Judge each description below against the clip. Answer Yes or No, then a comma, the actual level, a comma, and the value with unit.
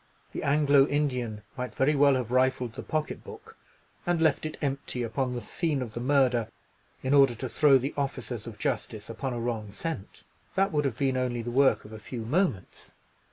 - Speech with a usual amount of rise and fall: Yes, average, 3.2 semitones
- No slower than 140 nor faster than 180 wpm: No, average, 200 wpm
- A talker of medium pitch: No, low, 130 Hz